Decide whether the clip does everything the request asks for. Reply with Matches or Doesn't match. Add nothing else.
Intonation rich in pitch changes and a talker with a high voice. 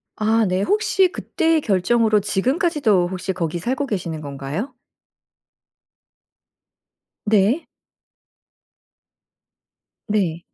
Matches